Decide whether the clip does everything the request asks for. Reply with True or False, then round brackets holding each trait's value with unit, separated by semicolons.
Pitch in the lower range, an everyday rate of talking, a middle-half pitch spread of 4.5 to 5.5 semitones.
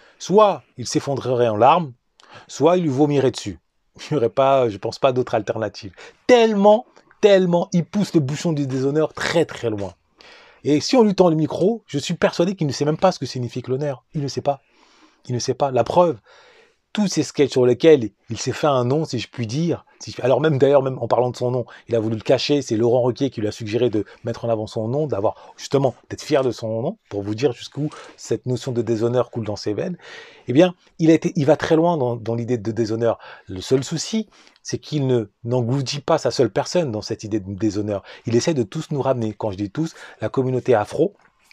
False (130 Hz; 235 wpm; 5.2 semitones)